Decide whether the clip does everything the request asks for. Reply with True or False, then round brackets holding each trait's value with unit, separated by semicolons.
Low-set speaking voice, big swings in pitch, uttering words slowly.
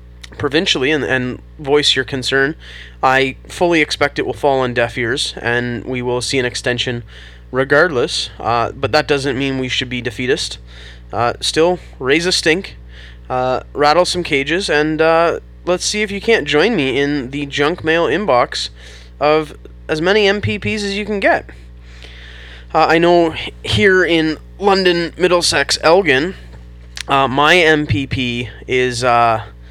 False (130 Hz; 7.7 semitones; 150 wpm)